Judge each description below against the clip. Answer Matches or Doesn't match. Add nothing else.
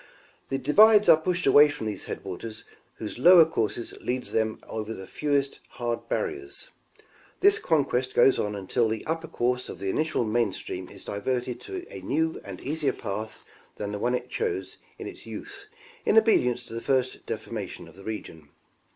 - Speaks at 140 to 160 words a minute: Doesn't match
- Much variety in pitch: Matches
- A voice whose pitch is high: Doesn't match